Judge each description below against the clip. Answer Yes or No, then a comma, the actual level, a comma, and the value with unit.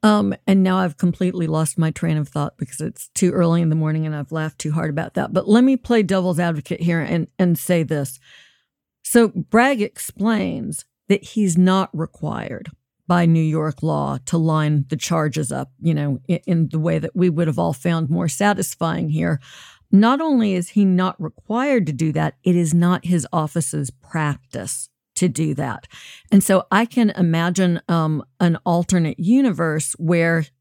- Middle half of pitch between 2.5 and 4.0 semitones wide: Yes, average, 3.1 semitones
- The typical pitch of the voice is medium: Yes, medium, 170 Hz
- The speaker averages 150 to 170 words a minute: No, average, 185 wpm